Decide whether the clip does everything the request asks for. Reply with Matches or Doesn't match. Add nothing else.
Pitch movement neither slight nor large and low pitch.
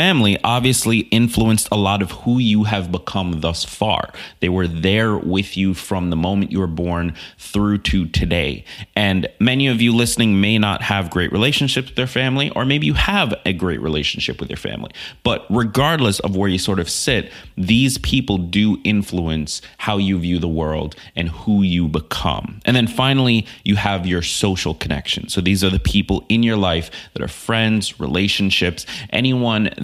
Matches